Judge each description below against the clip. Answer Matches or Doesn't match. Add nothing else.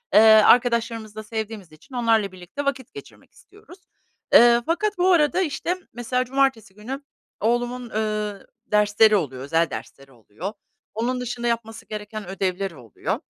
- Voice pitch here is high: Matches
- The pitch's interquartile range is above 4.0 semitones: Doesn't match